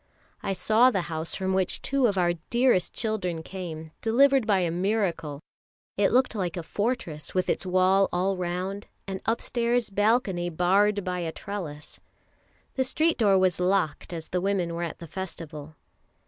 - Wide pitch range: No, average, 3.5 semitones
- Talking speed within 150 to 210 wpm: Yes, average, 165 wpm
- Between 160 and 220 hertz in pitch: Yes, high, 190 Hz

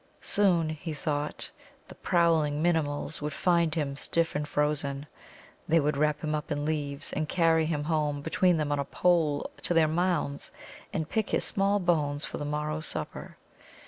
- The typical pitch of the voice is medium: Yes, medium, 155 Hz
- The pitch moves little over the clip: Yes, narrow, 2.2 semitones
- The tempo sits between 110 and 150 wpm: No, average, 175 wpm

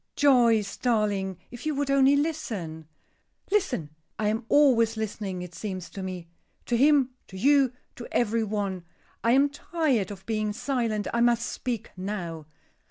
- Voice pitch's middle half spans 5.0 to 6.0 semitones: Yes, average, 5.3 semitones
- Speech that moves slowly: No, average, 155 wpm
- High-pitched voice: Yes, high, 225 Hz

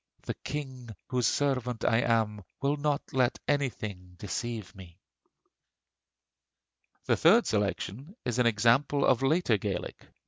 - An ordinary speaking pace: No, slow, 125 wpm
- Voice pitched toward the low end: Yes, low, 120 Hz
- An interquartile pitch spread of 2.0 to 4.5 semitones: No, average, 4.9 semitones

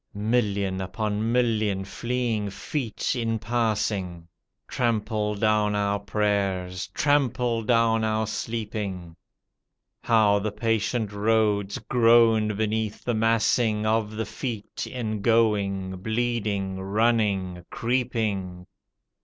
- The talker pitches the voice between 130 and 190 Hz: No, low, 110 Hz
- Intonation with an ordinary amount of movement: No, narrow, 2.1 semitones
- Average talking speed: No, slow, 105 wpm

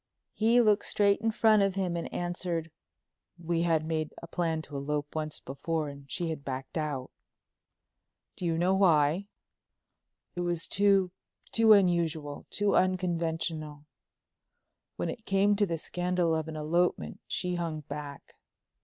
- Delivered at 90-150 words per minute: Yes, average, 140 wpm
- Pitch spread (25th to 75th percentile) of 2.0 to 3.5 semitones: Yes, average, 3.2 semitones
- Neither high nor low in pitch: Yes, medium, 170 Hz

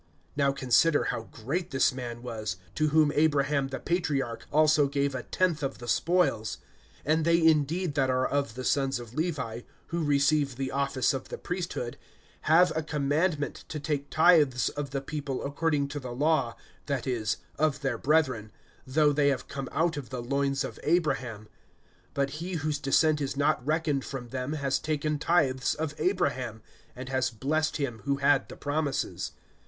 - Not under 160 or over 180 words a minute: Yes, average, 175 wpm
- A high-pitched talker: No, medium, 140 Hz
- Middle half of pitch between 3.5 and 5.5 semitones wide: No, average, 2.9 semitones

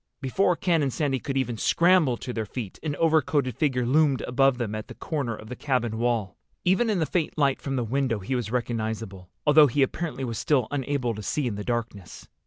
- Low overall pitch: Yes, low, 130 Hz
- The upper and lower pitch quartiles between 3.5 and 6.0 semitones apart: Yes, average, 4.2 semitones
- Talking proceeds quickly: Yes, fast, 215 wpm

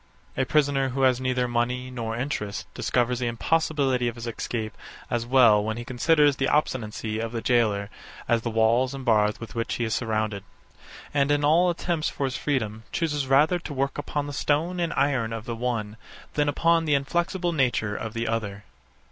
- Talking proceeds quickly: No, average, 190 wpm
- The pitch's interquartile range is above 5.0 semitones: No, average, 4.2 semitones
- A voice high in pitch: No, low, 125 Hz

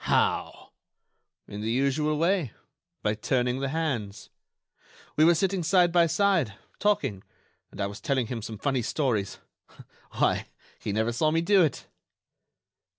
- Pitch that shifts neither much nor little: No, wide, 6.9 semitones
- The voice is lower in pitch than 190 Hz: Yes, low, 135 Hz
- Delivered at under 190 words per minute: Yes, average, 145 wpm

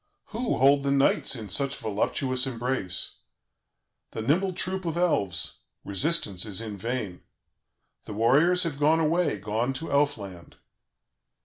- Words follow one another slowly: Yes, slow, 130 wpm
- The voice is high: No, low, 135 Hz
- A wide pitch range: Yes, wide, 7.1 semitones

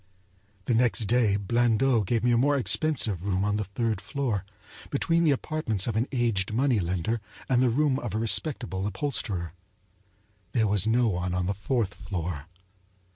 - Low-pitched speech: Yes, low, 110 Hz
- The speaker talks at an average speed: Yes, average, 170 wpm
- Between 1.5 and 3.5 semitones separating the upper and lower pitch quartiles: No, average, 4.3 semitones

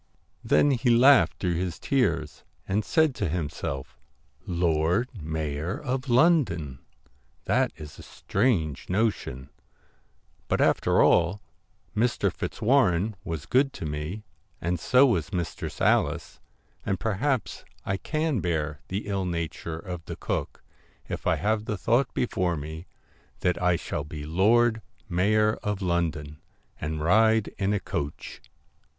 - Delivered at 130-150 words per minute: Yes, slow, 135 wpm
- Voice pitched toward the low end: Yes, very low, 90 Hz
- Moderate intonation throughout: No, wide, 5.8 semitones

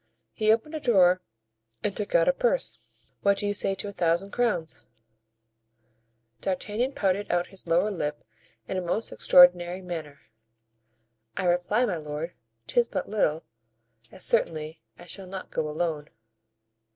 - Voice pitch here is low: No, medium, 185 Hz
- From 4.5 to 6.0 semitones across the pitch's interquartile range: No, average, 3.7 semitones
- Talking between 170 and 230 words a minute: No, average, 150 wpm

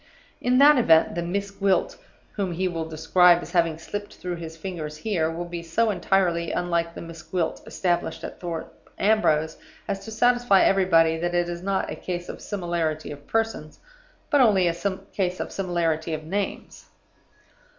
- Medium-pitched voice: Yes, medium, 175 Hz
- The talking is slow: No, average, 170 wpm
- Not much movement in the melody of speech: No, average, 3.1 semitones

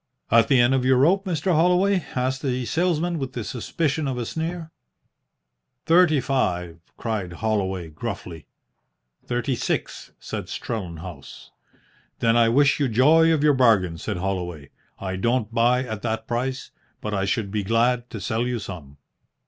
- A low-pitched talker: Yes, low, 120 Hz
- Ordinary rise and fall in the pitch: No, wide, 5.9 semitones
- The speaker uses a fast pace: No, average, 155 wpm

